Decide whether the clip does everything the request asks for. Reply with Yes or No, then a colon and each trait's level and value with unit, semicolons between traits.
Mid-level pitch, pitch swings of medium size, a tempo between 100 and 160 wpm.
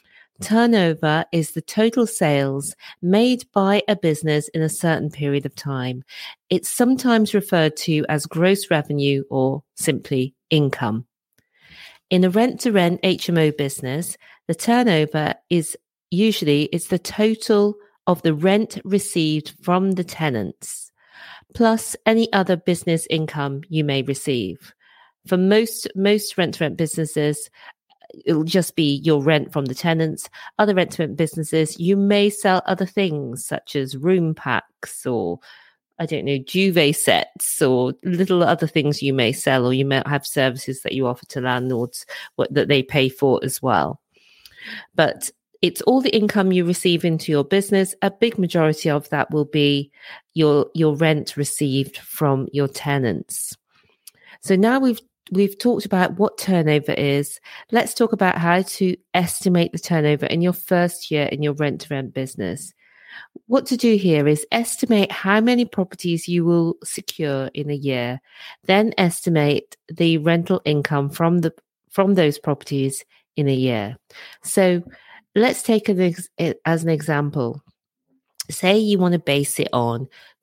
Yes: medium, 165 Hz; average, 4.9 semitones; average, 150 wpm